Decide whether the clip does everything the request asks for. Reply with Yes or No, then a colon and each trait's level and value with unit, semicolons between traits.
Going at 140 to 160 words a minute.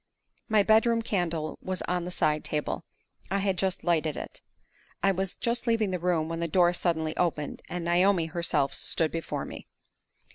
No: average, 175 wpm